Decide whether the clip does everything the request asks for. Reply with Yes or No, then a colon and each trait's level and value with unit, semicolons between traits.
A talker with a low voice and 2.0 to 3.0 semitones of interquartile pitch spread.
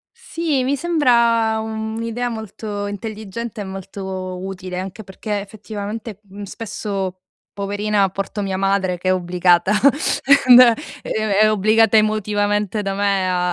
No: high, 205 Hz; narrow, 2.5 semitones